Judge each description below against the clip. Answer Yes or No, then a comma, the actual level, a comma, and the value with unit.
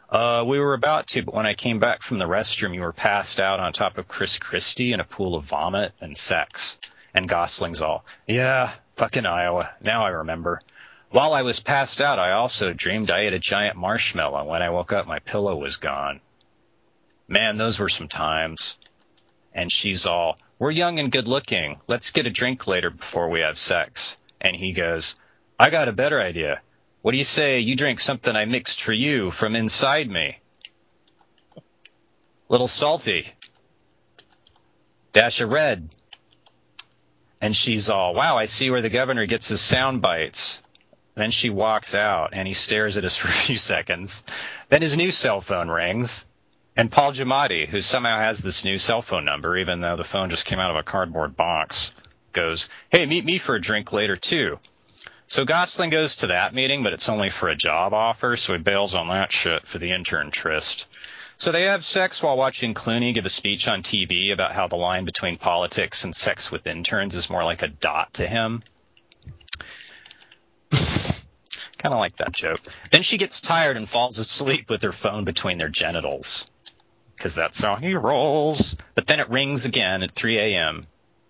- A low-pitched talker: Yes, low, 110 Hz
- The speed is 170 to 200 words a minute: Yes, average, 190 wpm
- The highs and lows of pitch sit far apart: Yes, wide, 6.2 semitones